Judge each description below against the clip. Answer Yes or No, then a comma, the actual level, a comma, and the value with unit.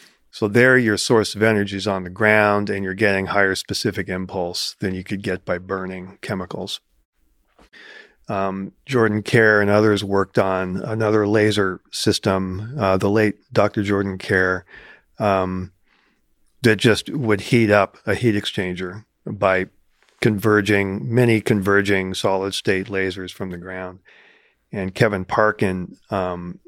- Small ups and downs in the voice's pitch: Yes, narrow, 2.2 semitones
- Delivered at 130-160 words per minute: Yes, average, 140 wpm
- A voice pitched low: Yes, low, 100 Hz